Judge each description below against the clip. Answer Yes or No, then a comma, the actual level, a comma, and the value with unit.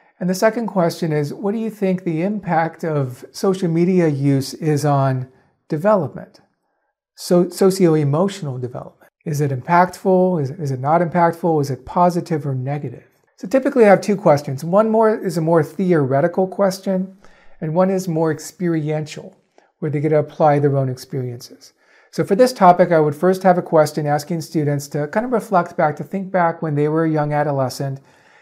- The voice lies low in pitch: No, medium, 165 Hz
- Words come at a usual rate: Yes, average, 180 wpm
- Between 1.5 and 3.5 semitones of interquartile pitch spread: No, average, 3.9 semitones